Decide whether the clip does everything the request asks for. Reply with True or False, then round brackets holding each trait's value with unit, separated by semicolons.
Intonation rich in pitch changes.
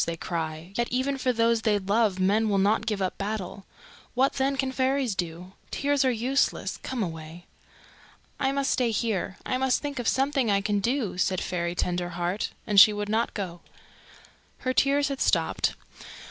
True (5.8 semitones)